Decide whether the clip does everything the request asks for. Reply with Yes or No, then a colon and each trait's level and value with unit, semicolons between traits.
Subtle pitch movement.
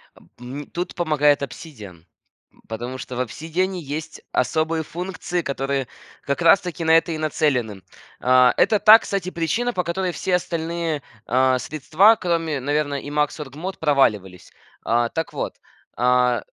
No: average, 5.0 semitones